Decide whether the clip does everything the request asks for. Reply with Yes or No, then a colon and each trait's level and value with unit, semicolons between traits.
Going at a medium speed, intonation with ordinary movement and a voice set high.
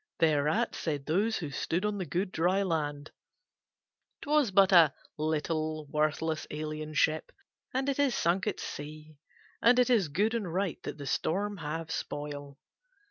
No: average, 155 wpm; average, 4.7 semitones; medium, 160 Hz